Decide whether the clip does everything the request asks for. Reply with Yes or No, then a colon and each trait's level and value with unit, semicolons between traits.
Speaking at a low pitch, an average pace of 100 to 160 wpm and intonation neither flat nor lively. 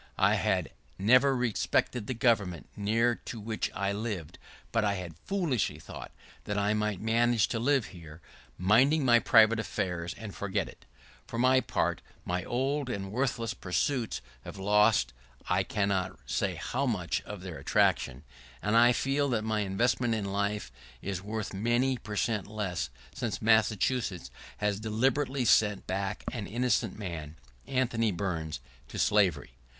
Yes: low, 105 Hz; average, 155 wpm; average, 3.6 semitones